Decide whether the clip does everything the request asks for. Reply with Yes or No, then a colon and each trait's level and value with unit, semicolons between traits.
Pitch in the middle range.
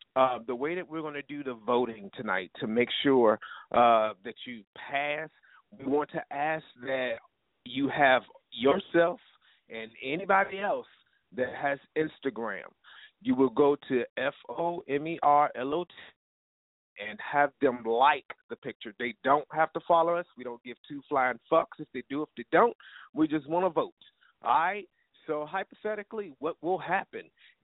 Yes: medium, 150 Hz